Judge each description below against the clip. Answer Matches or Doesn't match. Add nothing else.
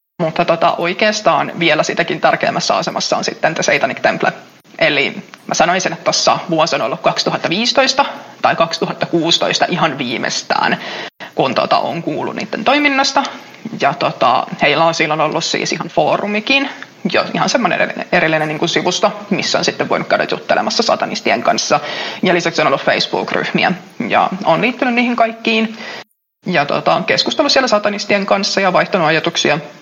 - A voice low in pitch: Doesn't match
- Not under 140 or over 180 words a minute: Matches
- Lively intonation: Matches